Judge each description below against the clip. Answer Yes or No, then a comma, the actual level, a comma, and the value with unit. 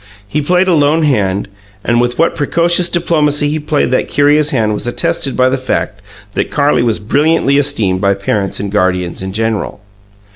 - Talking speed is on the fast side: No, average, 180 wpm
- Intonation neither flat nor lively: No, wide, 6.3 semitones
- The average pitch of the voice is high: No, low, 135 Hz